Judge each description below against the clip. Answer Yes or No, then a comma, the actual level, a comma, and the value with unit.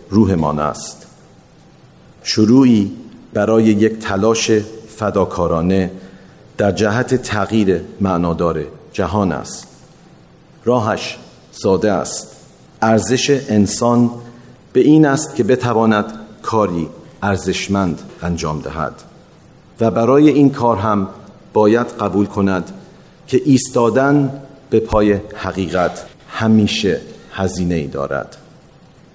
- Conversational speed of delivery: No, slow, 95 wpm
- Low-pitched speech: Yes, low, 105 Hz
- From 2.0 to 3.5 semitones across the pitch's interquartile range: No, average, 4.0 semitones